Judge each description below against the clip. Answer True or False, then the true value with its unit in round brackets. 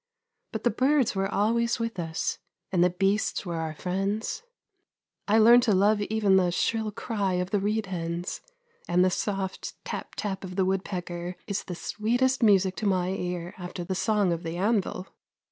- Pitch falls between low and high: False (195 Hz)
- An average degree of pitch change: True (3.1 semitones)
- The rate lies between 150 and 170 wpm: False (180 wpm)